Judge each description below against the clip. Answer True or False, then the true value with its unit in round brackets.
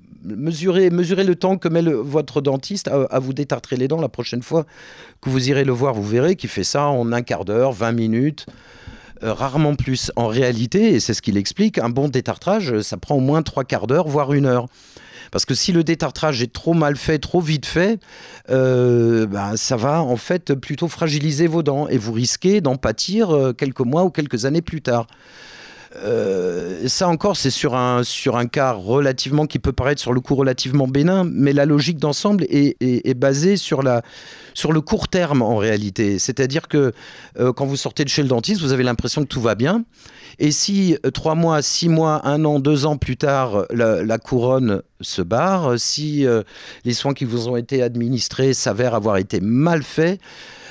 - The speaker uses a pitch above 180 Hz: False (140 Hz)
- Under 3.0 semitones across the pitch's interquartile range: False (4.3 semitones)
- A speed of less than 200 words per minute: False (205 wpm)